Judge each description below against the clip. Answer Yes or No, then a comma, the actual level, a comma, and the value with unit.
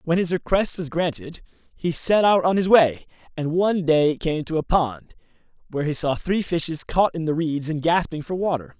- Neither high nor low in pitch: Yes, medium, 165 Hz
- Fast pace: Yes, fast, 210 wpm